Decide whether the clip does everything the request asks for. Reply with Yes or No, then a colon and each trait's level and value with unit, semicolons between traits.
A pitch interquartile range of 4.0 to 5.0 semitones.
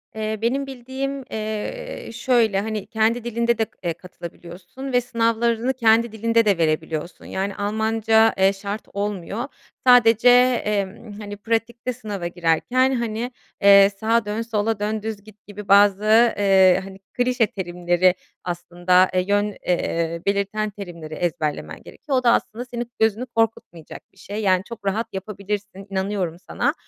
No: average, 3.2 semitones